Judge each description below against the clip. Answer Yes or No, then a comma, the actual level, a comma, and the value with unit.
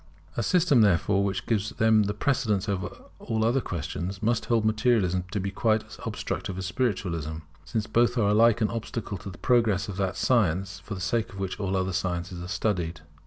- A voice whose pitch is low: Yes, low, 100 Hz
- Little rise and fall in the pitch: No, average, 3.4 semitones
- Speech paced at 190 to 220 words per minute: Yes, average, 200 wpm